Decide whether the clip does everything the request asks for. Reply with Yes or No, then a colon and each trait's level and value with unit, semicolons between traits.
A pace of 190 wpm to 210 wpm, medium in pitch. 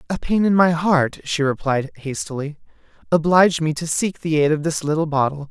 Yes: average, 195 wpm; medium, 155 Hz